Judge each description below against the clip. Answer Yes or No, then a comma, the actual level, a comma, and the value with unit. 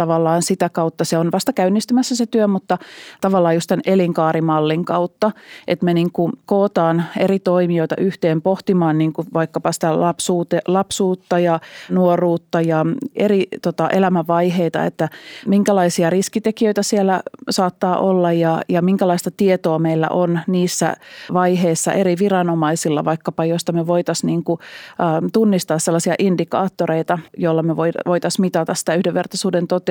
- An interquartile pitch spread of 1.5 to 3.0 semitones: Yes, narrow, 2.4 semitones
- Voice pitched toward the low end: No, medium, 175 Hz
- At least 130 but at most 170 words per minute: Yes, average, 140 wpm